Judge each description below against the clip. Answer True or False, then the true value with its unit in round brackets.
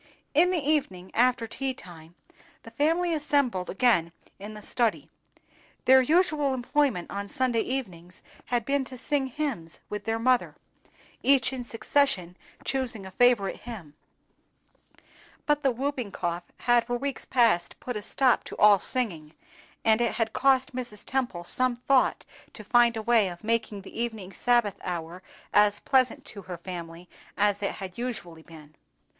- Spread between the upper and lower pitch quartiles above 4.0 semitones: True (5.4 semitones)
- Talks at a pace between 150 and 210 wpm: True (155 wpm)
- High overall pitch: True (235 Hz)